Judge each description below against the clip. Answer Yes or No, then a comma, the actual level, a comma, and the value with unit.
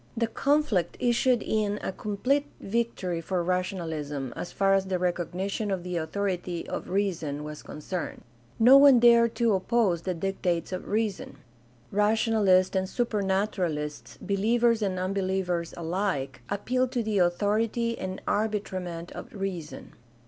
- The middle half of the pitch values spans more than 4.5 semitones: No, average, 3.8 semitones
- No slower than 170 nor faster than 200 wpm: No, slow, 135 wpm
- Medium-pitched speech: No, high, 195 Hz